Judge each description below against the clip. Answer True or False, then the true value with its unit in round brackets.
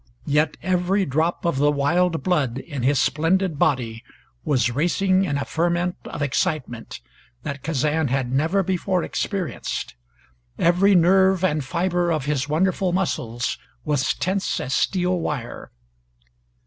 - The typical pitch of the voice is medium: True (160 Hz)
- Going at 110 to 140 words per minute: True (135 wpm)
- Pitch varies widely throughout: False (4.4 semitones)